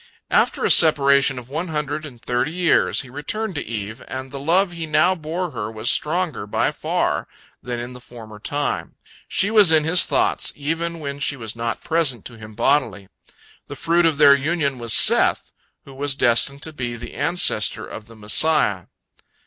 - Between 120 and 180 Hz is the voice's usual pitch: Yes, medium, 140 Hz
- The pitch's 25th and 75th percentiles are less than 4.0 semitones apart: No, average, 5.2 semitones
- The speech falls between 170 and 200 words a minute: Yes, average, 185 wpm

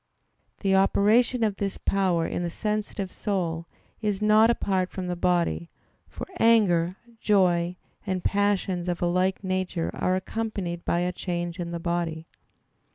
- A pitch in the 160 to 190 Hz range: Yes, medium, 185 Hz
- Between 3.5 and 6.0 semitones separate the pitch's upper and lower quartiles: No, average, 2.8 semitones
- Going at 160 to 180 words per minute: No, average, 150 wpm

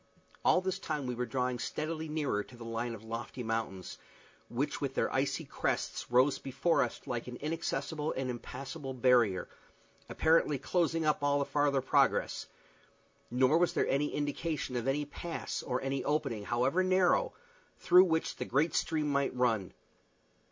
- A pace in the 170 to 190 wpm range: No, average, 160 wpm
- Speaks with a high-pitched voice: No, low, 135 Hz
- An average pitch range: Yes, average, 4.0 semitones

